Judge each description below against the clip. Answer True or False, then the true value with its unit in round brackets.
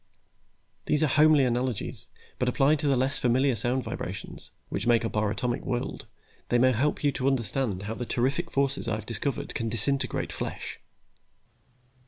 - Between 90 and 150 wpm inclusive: False (170 wpm)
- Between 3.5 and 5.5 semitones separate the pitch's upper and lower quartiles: False (2.8 semitones)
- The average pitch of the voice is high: False (130 Hz)